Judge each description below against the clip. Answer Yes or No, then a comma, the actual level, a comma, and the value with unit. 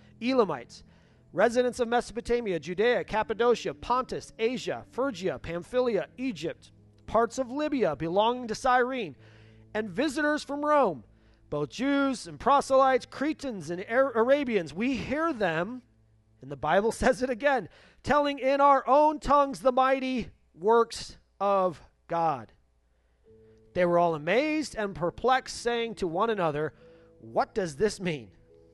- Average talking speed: No, slow, 125 wpm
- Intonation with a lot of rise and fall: Yes, wide, 7.8 semitones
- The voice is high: Yes, high, 225 Hz